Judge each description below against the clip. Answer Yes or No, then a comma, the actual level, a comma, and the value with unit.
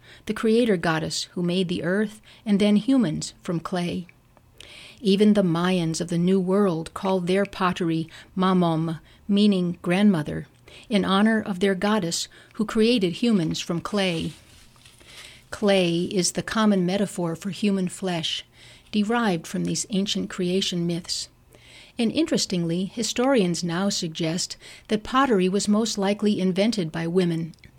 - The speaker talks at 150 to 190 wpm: No, slow, 135 wpm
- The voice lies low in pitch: No, medium, 185 Hz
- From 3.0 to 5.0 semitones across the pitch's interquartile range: Yes, average, 3.3 semitones